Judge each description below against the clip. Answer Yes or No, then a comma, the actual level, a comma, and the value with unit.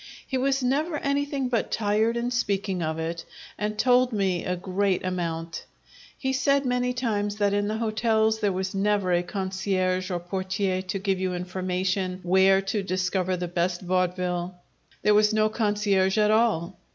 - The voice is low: No, high, 195 Hz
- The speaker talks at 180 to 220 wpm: No, average, 165 wpm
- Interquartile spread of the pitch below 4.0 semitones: Yes, average, 3.1 semitones